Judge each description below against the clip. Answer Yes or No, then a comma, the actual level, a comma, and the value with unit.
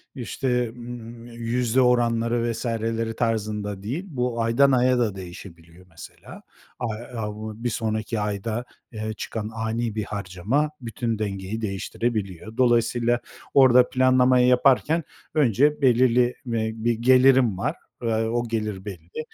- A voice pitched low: Yes, low, 115 Hz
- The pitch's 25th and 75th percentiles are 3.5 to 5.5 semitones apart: No, narrow, 2.4 semitones